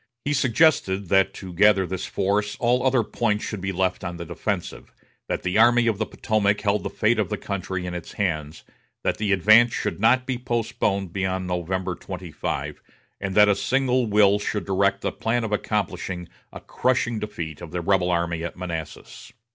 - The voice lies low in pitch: Yes, low, 100 Hz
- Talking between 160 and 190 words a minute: Yes, average, 185 wpm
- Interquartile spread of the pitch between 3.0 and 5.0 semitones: Yes, average, 3.4 semitones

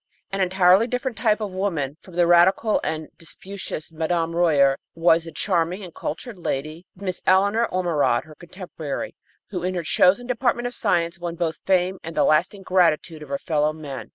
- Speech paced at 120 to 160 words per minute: No, average, 175 wpm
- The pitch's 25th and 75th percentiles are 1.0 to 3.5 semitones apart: Yes, average, 3.2 semitones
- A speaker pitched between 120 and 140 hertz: No, medium, 175 Hz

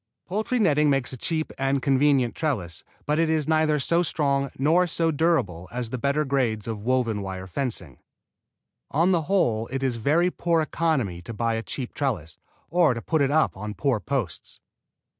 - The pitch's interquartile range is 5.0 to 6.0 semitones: Yes, wide, 5.5 semitones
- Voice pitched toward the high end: No, medium, 140 Hz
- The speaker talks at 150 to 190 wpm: Yes, average, 180 wpm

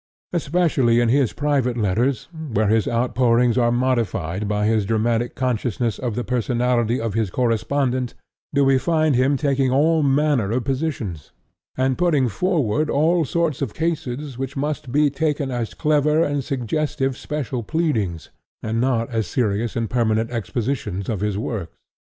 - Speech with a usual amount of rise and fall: Yes, average, 4.0 semitones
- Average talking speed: Yes, average, 150 wpm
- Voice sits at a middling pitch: No, low, 125 Hz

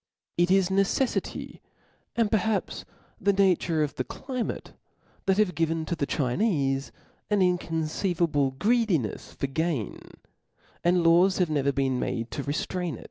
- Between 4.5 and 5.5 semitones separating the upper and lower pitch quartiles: Yes, average, 5.2 semitones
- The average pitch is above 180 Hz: No, medium, 170 Hz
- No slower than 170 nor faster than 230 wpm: No, slow, 135 wpm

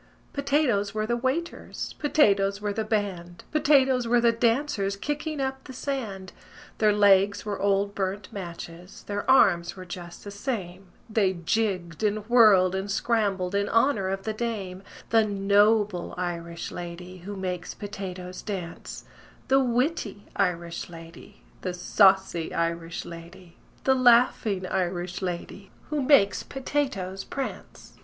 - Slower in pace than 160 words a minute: Yes, slow, 135 wpm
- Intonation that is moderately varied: Yes, average, 4.2 semitones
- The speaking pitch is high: Yes, high, 200 Hz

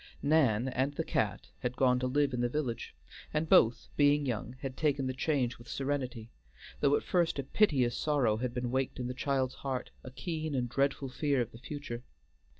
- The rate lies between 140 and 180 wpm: No, average, 200 wpm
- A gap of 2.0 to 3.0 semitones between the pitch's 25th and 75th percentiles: Yes, average, 2.7 semitones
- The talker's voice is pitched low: Yes, low, 130 Hz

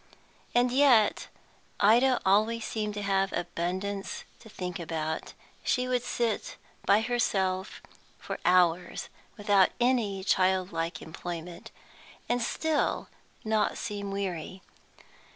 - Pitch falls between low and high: No, high, 200 Hz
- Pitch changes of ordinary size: Yes, average, 4.1 semitones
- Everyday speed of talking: No, slow, 105 wpm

